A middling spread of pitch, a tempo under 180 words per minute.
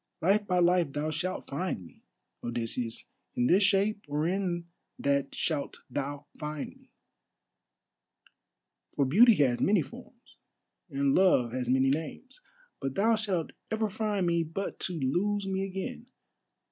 No: wide, 6.1 semitones; slow, 135 wpm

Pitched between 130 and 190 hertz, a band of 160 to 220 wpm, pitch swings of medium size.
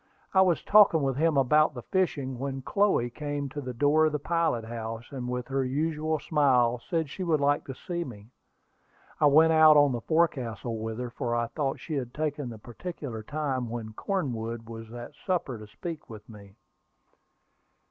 Yes: low, 135 Hz; average, 190 wpm; average, 4.8 semitones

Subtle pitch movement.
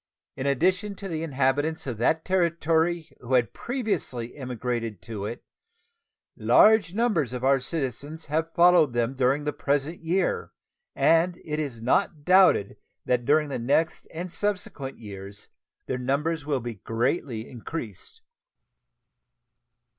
No: average, 5.3 semitones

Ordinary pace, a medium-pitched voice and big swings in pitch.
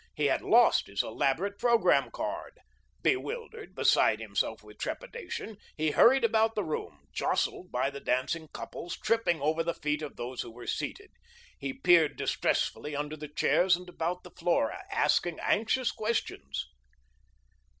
Yes: average, 150 wpm; medium, 175 Hz; wide, 7.5 semitones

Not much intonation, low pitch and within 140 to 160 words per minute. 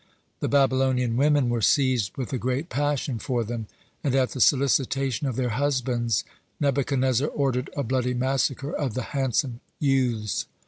Yes: narrow, 2.1 semitones; low, 130 Hz; average, 150 wpm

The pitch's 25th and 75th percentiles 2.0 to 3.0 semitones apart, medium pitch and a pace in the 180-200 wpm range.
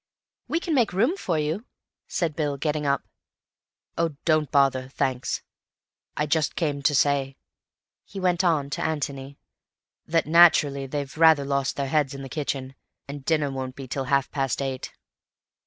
No: average, 2.7 semitones; medium, 145 Hz; average, 160 wpm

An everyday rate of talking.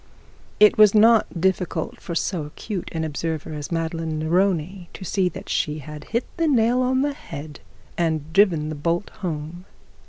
Yes: average, 165 wpm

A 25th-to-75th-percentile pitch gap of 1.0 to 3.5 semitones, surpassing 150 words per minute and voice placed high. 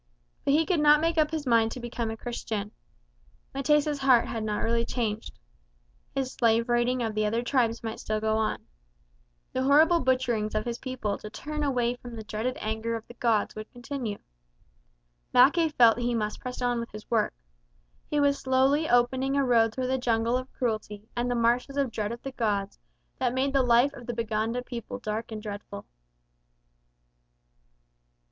Yes: average, 2.8 semitones; average, 180 wpm; high, 240 Hz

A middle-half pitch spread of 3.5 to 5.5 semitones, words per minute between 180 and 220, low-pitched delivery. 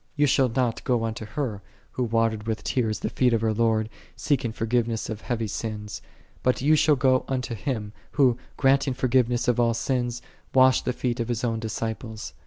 No: narrow, 2.5 semitones; average, 195 wpm; low, 120 Hz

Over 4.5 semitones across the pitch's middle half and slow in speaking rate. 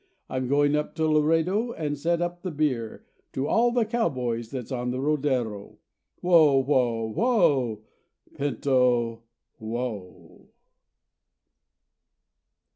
Yes: average, 5.0 semitones; slow, 110 wpm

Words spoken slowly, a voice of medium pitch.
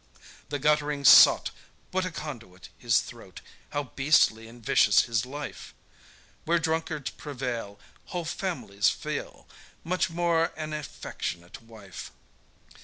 Yes: slow, 115 wpm; medium, 145 Hz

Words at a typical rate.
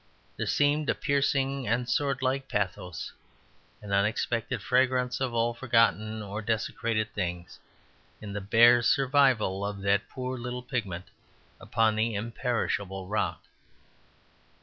No: slow, 120 wpm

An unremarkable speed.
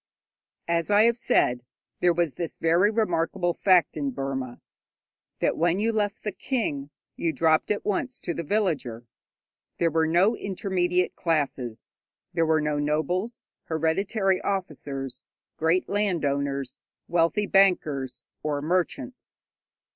No: slow, 130 wpm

